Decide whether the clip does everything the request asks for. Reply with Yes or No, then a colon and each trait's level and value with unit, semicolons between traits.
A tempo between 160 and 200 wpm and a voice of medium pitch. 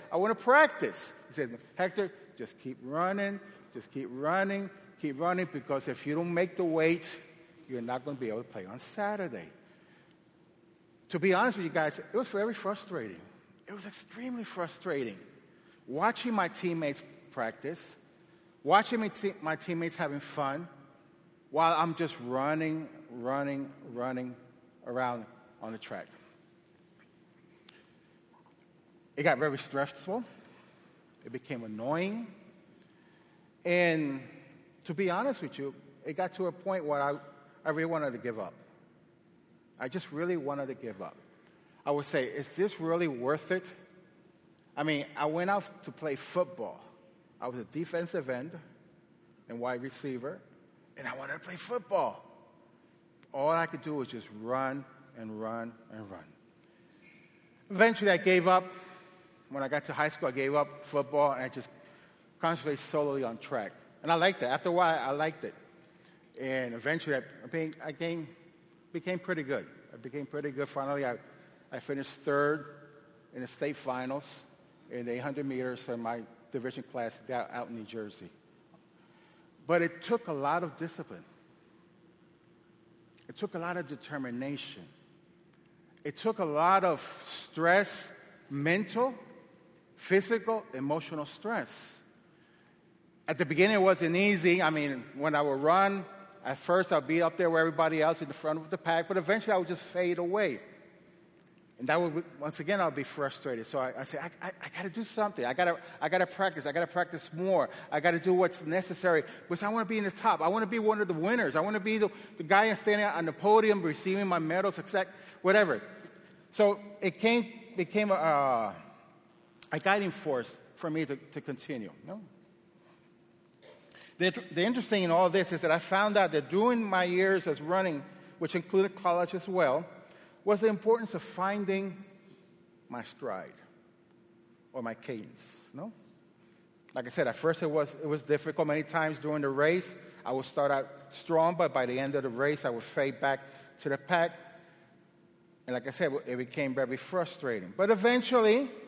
Yes: average, 170 wpm; medium, 170 Hz